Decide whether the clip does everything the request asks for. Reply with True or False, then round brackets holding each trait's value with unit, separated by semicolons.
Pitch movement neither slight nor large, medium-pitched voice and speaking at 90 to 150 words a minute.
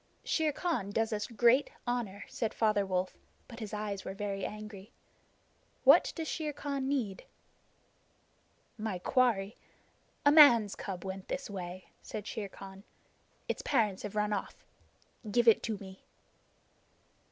False (3.7 semitones; 210 Hz; 140 wpm)